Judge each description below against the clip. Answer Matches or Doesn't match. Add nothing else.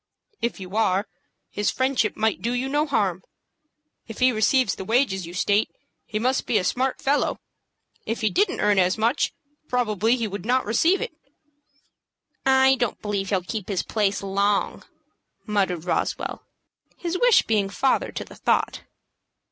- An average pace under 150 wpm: Doesn't match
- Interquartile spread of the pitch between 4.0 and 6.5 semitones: Matches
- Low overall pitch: Doesn't match